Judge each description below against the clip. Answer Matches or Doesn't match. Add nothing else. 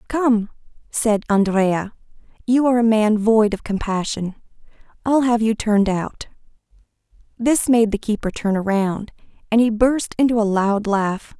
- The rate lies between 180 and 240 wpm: Doesn't match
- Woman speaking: Matches